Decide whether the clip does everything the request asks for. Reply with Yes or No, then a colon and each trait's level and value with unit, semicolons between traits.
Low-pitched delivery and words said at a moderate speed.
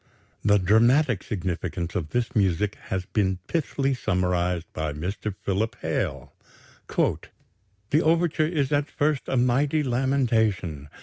No: low, 105 Hz; slow, 120 wpm